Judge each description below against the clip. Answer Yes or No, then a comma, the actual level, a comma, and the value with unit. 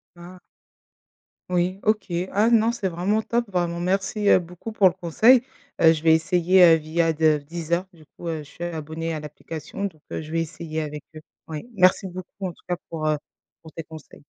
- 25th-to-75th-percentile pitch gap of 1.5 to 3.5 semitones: Yes, average, 2.8 semitones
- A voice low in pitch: No, medium, 170 Hz